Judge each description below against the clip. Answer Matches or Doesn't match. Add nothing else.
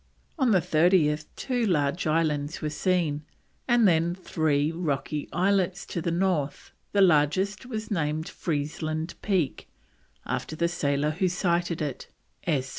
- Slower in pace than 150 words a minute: Matches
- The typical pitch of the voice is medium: Matches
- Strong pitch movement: Doesn't match